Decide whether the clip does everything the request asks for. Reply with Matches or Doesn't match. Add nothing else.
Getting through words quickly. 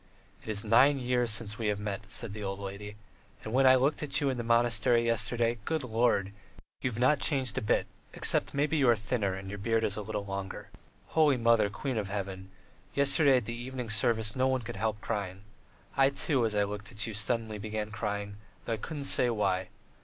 Matches